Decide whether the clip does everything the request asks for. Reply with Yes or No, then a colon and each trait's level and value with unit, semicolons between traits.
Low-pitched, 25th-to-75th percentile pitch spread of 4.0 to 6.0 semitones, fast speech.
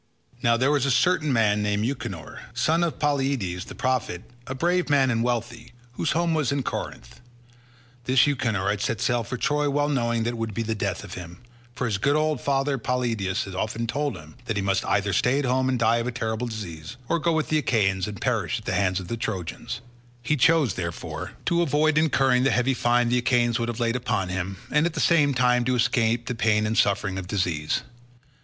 Yes: low, 120 Hz; average, 4.7 semitones; fast, 220 wpm